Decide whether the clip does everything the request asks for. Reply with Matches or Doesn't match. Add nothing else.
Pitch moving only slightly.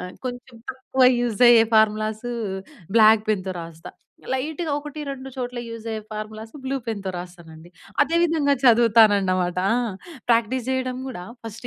Doesn't match